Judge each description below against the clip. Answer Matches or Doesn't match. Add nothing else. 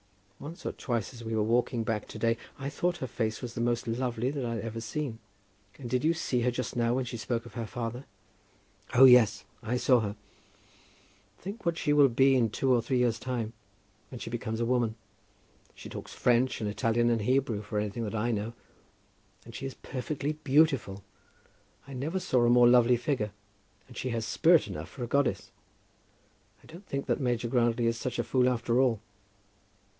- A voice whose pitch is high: Doesn't match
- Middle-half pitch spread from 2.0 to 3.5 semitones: Matches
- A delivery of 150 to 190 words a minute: Doesn't match